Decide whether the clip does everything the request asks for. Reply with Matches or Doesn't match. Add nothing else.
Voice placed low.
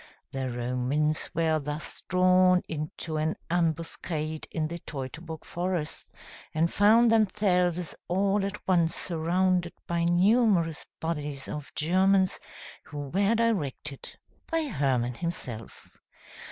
Doesn't match